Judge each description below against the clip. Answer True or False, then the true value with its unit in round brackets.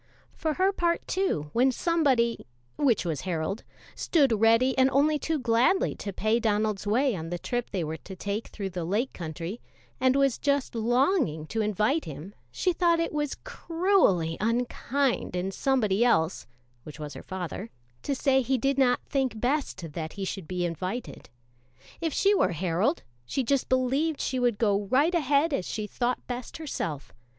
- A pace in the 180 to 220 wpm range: False (170 wpm)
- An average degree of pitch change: False (6.6 semitones)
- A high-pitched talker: True (235 Hz)